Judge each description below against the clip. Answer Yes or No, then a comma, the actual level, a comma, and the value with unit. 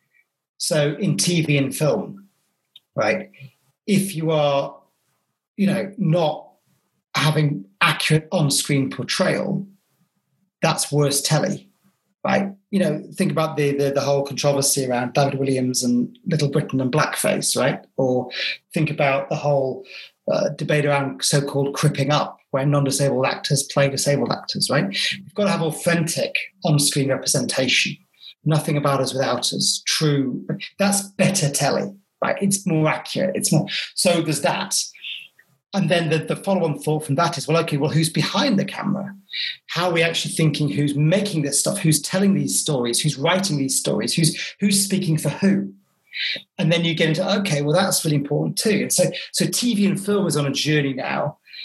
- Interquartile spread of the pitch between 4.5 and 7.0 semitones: Yes, average, 4.9 semitones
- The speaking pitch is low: No, medium, 160 Hz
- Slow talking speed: No, average, 170 wpm